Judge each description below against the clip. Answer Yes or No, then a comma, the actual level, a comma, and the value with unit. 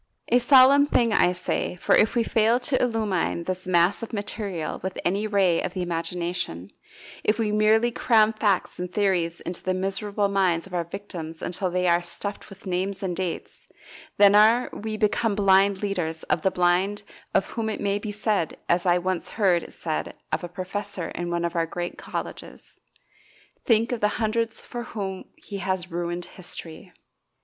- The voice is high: Yes, high, 195 Hz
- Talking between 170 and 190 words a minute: Yes, average, 180 wpm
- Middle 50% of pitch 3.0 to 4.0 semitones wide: Yes, average, 3.3 semitones